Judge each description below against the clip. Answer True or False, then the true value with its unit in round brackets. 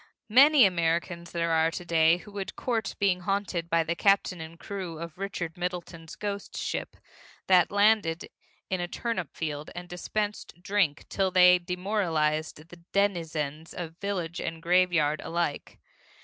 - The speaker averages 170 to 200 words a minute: False (150 wpm)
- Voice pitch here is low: False (175 Hz)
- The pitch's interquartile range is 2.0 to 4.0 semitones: True (3.1 semitones)